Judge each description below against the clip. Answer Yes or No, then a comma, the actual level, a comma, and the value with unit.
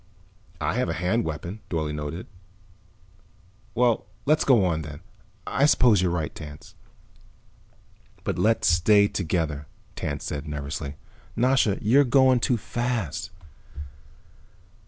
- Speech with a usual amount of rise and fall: No, wide, 7.6 semitones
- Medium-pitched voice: No, very low, 90 Hz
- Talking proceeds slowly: Yes, slow, 115 wpm